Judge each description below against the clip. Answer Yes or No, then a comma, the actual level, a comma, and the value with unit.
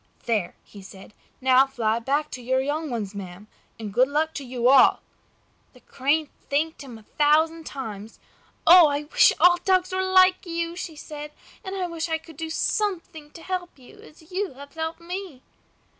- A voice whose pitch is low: No, very high, 300 Hz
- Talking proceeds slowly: No, average, 180 wpm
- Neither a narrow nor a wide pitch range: Yes, average, 4.9 semitones